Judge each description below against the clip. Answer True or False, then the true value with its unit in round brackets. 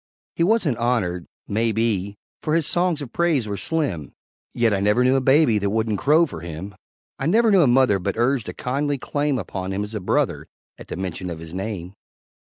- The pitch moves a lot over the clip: True (6.6 semitones)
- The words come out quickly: True (210 wpm)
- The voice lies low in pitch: True (115 Hz)